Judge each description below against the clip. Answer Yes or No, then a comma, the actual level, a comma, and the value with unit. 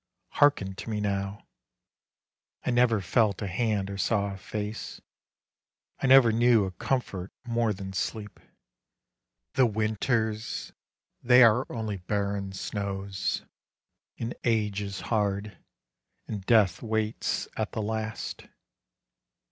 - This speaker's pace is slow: Yes, slow, 115 wpm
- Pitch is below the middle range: Yes, low, 105 Hz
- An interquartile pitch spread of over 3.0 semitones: No, narrow, 2.5 semitones